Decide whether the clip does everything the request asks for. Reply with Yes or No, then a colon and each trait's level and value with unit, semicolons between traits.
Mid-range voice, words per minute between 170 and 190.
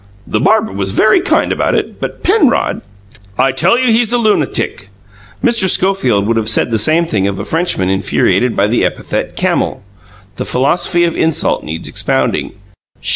Yes: medium, 155 Hz; average, 175 wpm